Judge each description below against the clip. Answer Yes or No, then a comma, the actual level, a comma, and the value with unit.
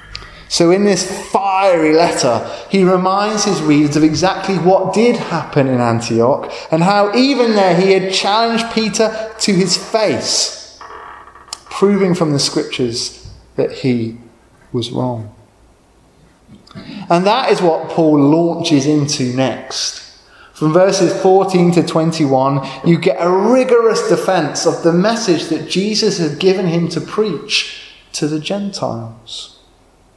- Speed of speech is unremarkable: No, slow, 130 wpm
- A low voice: No, medium, 170 Hz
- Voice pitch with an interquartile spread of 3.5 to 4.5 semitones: No, average, 5.2 semitones